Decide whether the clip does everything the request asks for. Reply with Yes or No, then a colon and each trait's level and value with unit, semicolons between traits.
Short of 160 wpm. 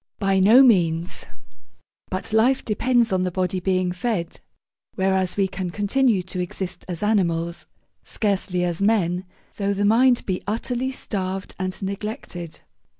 Yes: average, 140 wpm